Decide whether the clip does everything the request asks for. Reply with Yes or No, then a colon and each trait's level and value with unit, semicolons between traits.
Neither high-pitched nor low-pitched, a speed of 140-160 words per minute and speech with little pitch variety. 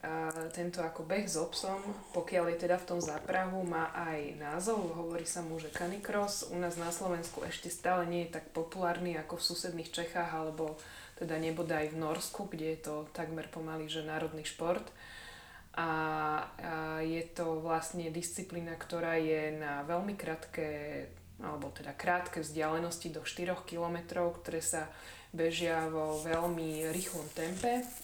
Yes: medium, 165 Hz; average, 155 wpm; narrow, 1.6 semitones